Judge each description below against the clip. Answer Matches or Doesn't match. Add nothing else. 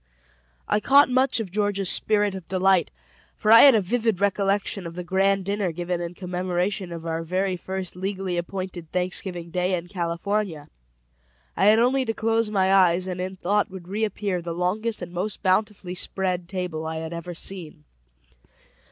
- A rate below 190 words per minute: Matches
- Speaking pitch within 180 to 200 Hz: Matches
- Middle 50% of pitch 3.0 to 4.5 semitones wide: Doesn't match